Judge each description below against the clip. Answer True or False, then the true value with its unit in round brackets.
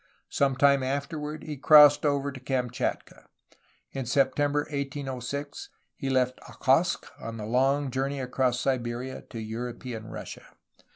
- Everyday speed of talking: False (125 wpm)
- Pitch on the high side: False (135 Hz)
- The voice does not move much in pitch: True (2.3 semitones)